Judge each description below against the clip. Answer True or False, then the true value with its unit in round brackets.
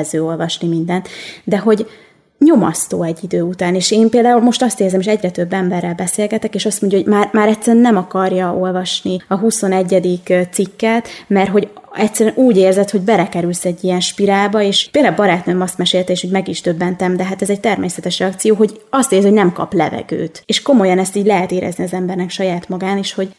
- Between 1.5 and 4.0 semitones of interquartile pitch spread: True (2.8 semitones)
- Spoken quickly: True (200 wpm)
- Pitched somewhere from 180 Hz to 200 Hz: True (190 Hz)